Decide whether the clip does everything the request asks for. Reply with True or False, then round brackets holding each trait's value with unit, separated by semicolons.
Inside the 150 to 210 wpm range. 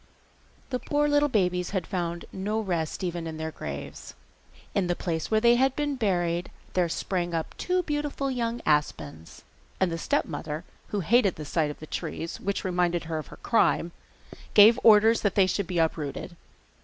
True (180 wpm)